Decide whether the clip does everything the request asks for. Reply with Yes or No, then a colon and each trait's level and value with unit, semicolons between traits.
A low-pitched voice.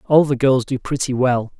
Yes: low, 130 Hz